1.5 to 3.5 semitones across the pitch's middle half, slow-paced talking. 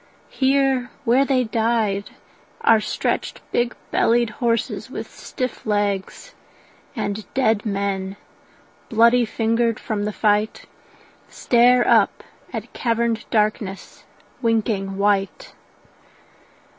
Yes: average, 2.7 semitones; slow, 95 wpm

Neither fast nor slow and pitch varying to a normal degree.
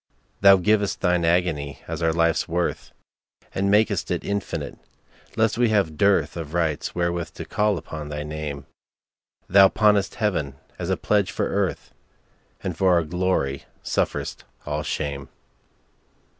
No: slow, 130 wpm; average, 4.5 semitones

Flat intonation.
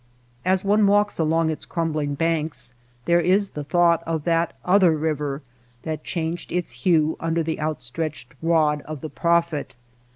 Yes: narrow, 2.0 semitones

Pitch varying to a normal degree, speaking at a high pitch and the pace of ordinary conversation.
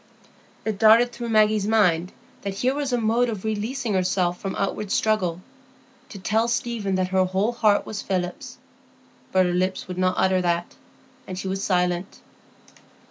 Yes: average, 3.4 semitones; high, 200 Hz; average, 160 wpm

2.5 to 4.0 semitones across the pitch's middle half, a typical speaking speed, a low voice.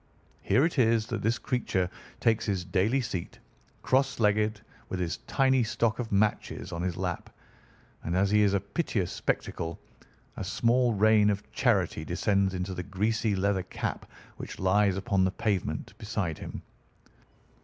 Yes: average, 3.3 semitones; average, 155 wpm; low, 100 Hz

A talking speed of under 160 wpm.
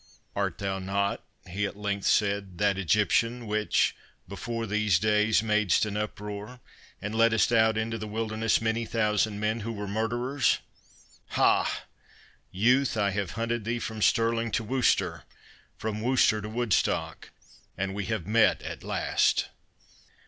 Yes: average, 140 wpm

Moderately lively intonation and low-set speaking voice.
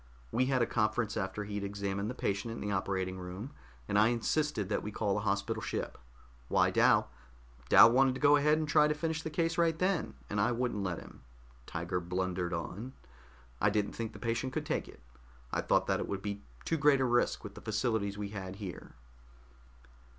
Yes: average, 4.7 semitones; low, 110 Hz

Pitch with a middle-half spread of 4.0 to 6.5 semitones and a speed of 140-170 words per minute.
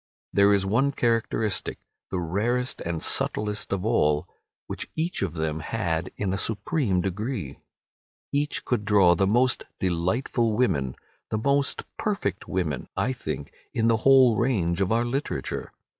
Yes: average, 5.2 semitones; average, 145 wpm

